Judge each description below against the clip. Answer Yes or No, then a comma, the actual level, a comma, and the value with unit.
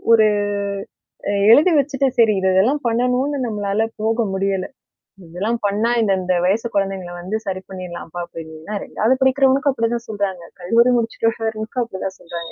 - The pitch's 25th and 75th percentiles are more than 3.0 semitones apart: Yes, average, 3.8 semitones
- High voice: Yes, high, 215 Hz